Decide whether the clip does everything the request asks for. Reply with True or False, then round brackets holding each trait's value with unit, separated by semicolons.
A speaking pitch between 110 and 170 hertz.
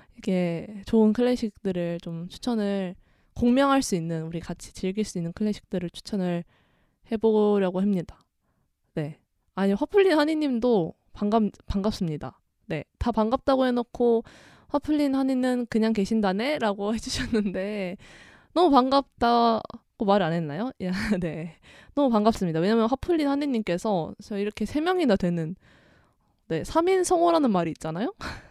False (215 Hz)